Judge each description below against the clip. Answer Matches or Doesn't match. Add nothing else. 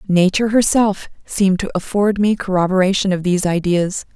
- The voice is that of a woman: Matches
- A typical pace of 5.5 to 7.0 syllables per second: Matches